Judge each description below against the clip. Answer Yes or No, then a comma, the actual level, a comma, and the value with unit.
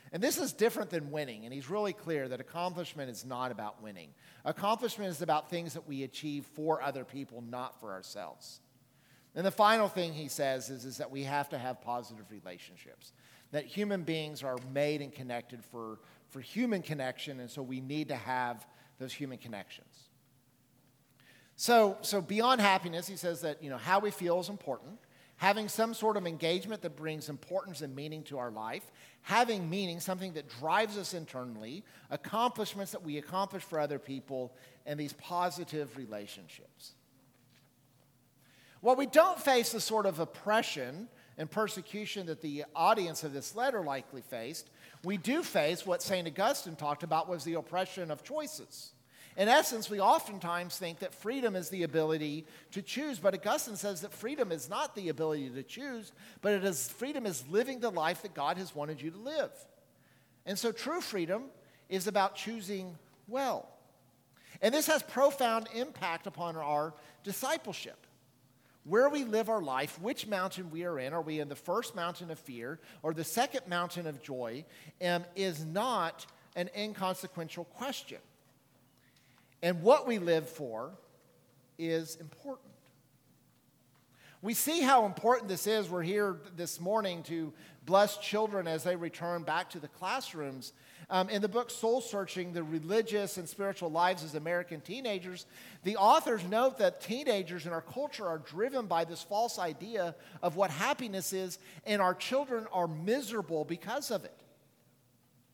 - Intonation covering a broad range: Yes, wide, 6.6 semitones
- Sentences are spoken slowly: No, average, 165 wpm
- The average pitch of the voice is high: No, medium, 170 Hz